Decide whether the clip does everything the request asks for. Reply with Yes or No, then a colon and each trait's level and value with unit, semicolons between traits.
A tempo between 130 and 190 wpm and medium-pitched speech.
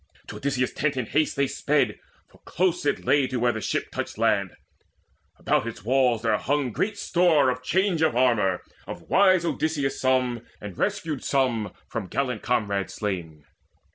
No: average, 170 wpm; low, 130 Hz